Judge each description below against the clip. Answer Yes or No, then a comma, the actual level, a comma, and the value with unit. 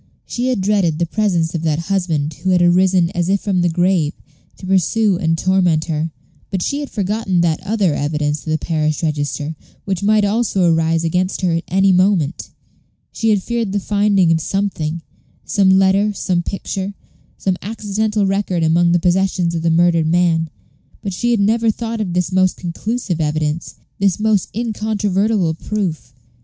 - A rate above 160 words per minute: Yes, average, 170 wpm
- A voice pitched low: No, medium, 185 Hz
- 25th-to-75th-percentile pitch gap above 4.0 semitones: No, average, 3.6 semitones